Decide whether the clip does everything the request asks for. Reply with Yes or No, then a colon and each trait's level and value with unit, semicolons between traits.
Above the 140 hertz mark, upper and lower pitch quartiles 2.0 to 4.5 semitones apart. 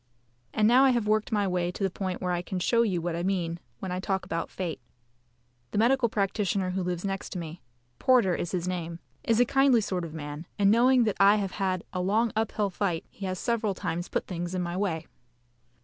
Yes: high, 190 Hz; average, 3.4 semitones